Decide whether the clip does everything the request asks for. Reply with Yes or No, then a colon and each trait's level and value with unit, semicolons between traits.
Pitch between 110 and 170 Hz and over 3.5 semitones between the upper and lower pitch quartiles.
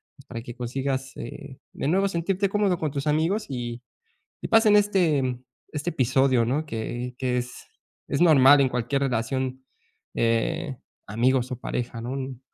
Yes: low, 135 Hz; average, 4.2 semitones